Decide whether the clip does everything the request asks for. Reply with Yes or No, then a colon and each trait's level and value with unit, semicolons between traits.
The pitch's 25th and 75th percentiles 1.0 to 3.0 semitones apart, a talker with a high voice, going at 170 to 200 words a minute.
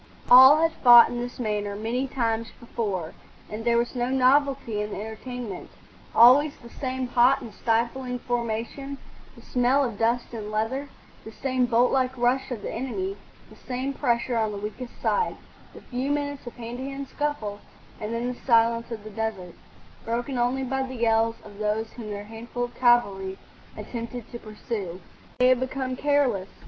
Yes: average, 2.7 semitones; high, 240 Hz; average, 175 wpm